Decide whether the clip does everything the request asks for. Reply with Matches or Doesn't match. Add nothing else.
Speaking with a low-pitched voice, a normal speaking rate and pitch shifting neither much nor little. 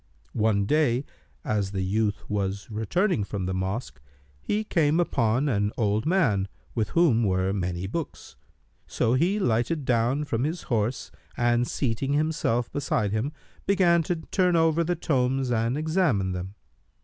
Doesn't match